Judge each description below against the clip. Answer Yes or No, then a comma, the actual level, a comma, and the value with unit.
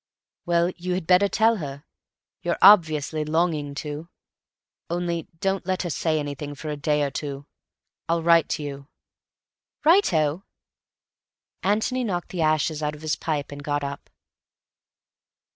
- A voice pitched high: No, medium, 160 Hz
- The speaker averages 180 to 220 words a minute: No, average, 145 wpm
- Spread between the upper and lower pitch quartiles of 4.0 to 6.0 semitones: No, average, 3.4 semitones